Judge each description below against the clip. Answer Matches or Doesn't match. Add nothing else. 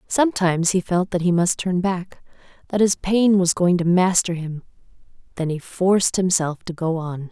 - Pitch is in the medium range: Matches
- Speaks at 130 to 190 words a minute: Matches